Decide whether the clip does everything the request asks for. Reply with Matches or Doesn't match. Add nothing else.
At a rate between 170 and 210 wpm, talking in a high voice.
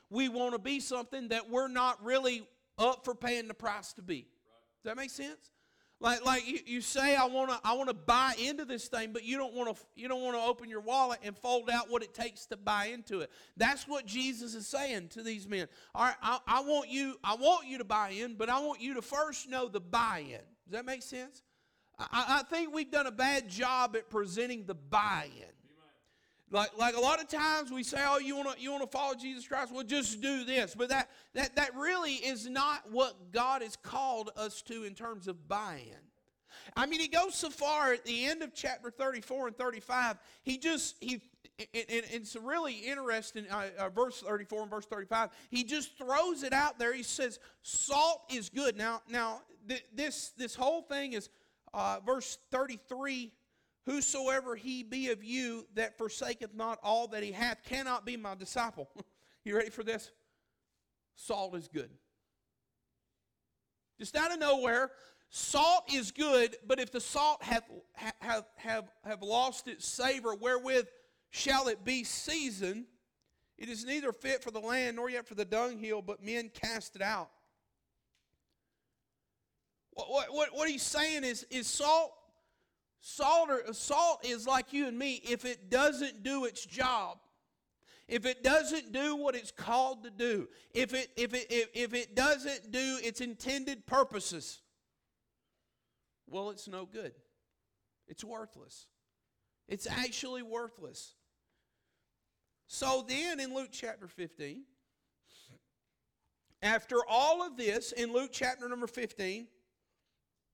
Matches